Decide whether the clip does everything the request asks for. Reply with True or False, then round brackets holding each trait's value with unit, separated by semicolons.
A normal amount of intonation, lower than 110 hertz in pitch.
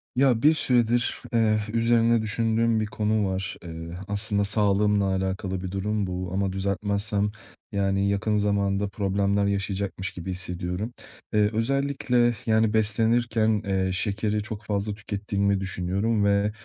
False (2.1 semitones; 100 Hz)